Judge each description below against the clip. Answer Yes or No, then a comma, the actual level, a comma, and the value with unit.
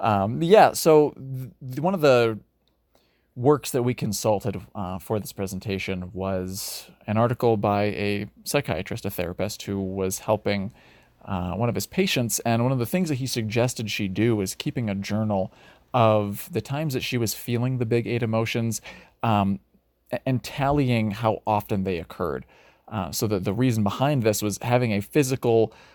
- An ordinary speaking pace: Yes, average, 170 wpm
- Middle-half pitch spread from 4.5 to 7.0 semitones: No, average, 3.8 semitones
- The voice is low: Yes, low, 110 Hz